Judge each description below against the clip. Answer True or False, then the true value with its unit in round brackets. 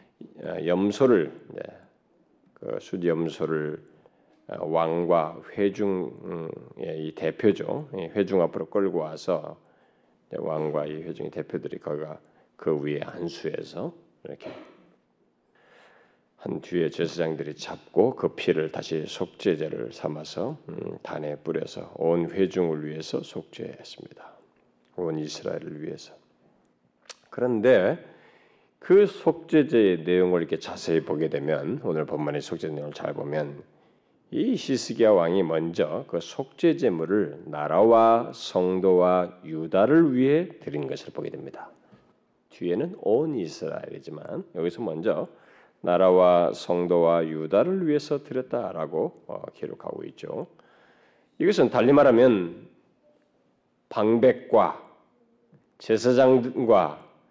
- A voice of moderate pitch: False (90 Hz)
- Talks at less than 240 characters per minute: True (230 characters per minute)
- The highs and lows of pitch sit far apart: True (7.6 semitones)